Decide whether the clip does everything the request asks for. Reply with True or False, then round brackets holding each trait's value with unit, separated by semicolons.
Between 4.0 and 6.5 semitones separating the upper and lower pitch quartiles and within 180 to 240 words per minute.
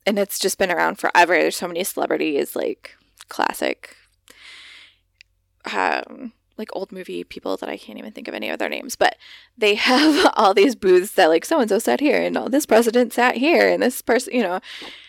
True (5.1 semitones; 200 wpm)